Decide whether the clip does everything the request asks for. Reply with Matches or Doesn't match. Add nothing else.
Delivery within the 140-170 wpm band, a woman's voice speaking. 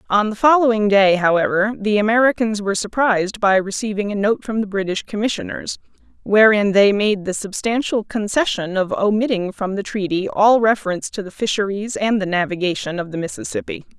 Matches